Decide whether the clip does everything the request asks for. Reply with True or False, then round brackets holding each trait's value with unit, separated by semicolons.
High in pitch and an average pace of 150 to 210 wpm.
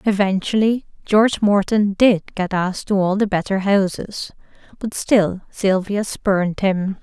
False (200 Hz; 135 wpm)